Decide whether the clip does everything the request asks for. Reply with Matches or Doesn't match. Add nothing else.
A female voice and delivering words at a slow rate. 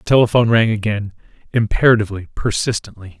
Doesn't match